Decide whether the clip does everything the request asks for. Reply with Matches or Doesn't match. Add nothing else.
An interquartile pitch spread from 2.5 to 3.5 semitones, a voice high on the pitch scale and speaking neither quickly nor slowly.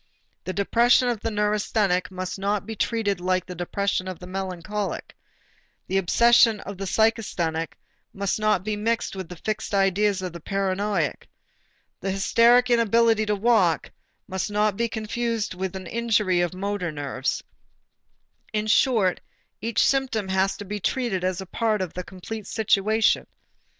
Matches